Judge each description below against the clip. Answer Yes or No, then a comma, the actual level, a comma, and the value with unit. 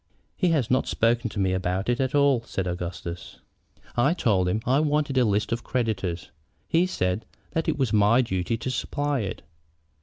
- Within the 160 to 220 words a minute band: Yes, average, 190 wpm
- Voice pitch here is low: Yes, low, 115 Hz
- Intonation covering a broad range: Yes, wide, 6.1 semitones